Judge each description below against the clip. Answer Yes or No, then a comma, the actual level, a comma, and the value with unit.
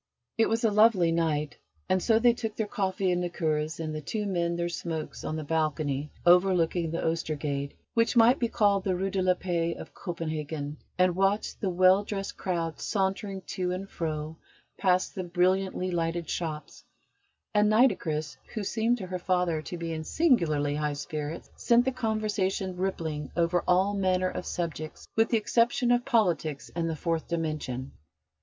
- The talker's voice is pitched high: No, medium, 180 Hz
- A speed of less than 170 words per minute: No, average, 175 wpm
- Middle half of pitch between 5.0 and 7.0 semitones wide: No, average, 3.8 semitones